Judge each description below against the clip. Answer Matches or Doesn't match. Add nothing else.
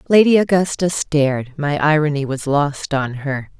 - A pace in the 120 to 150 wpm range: Matches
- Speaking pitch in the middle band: Matches